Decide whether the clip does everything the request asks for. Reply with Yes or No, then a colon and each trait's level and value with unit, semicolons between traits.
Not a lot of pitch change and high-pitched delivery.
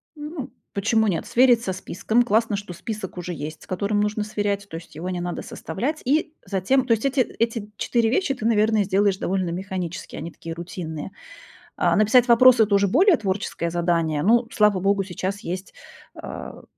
No: average, 4.2 semitones; high, 205 Hz